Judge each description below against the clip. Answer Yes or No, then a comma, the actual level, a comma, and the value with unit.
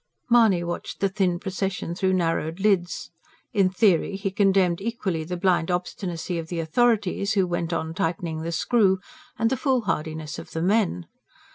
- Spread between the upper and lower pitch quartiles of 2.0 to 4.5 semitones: Yes, average, 2.9 semitones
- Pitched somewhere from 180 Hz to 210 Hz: Yes, medium, 185 Hz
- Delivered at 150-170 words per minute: Yes, average, 160 wpm